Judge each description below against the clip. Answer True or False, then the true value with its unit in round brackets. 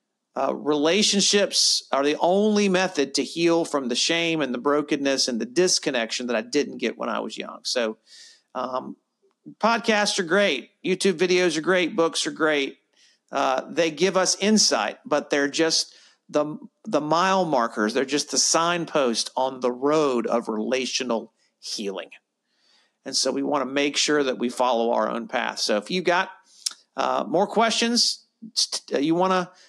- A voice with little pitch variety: False (5.0 semitones)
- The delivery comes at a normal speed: True (165 wpm)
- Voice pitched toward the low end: False (165 Hz)